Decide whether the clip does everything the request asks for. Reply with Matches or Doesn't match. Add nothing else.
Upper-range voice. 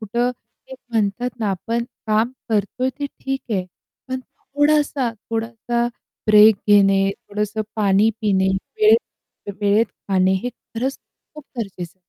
Matches